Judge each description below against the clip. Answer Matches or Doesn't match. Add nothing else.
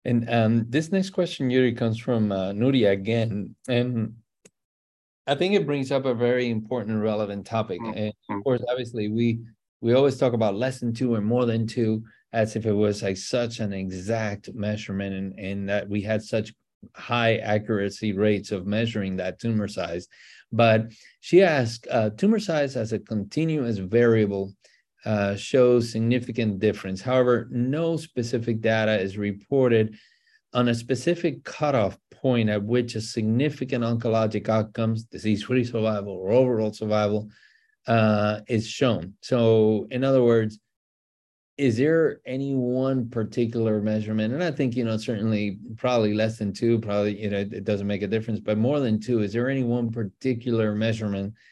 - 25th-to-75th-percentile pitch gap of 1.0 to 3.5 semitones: Matches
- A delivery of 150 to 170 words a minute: Matches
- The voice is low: Matches